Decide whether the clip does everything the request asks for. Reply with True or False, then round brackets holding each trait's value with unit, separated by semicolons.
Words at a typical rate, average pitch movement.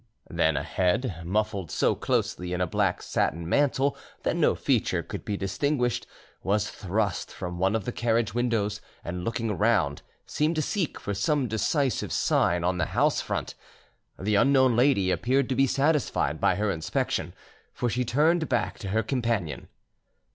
False (165 wpm; 5.8 semitones)